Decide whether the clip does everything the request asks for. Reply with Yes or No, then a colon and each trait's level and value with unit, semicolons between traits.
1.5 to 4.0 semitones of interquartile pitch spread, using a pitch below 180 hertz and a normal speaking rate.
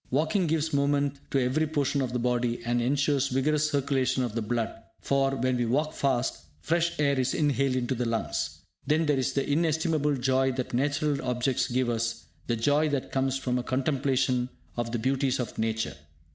Yes: average, 2.7 semitones; low, 135 Hz; average, 185 wpm